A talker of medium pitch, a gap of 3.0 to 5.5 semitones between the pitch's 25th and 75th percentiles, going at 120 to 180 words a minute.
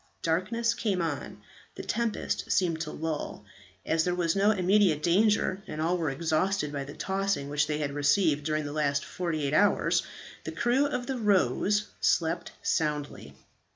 Yes: medium, 165 Hz; average, 4.8 semitones; average, 165 wpm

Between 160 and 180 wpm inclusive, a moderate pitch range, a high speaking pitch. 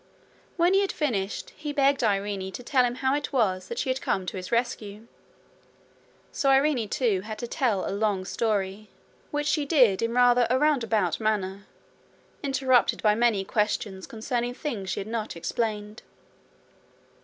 Yes: average, 165 wpm; average, 4.5 semitones; high, 230 Hz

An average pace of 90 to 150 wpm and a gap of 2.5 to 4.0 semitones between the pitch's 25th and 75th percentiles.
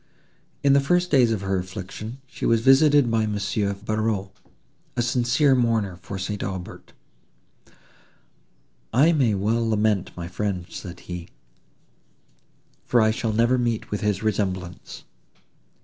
Yes: slow, 135 wpm; average, 3.7 semitones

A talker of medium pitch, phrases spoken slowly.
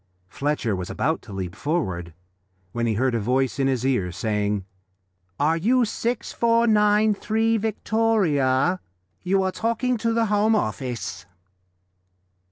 Yes: medium, 155 Hz; slow, 125 wpm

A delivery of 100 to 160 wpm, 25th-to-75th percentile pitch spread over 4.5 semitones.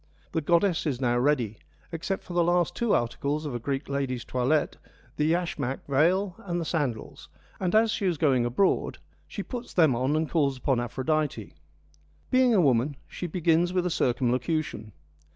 No: average, 170 wpm; average, 5.3 semitones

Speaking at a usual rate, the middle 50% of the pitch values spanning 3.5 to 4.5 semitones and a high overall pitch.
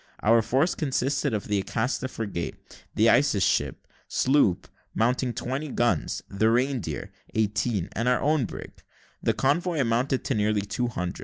No: average, 150 wpm; average, 4.0 semitones; low, 120 Hz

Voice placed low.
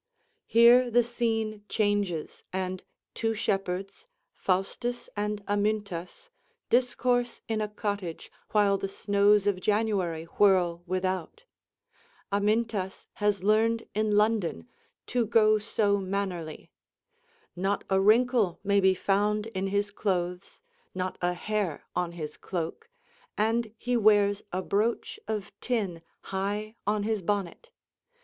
No: high, 205 Hz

